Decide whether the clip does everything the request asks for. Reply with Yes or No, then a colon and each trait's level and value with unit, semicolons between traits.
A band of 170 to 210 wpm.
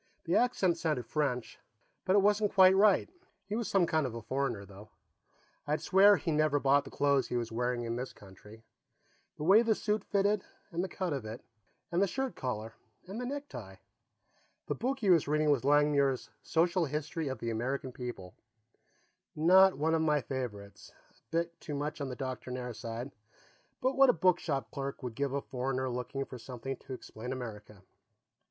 Yes: average, 185 wpm